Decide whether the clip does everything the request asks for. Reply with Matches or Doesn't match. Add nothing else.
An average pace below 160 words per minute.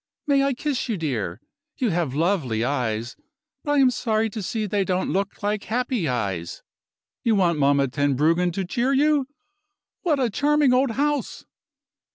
Doesn't match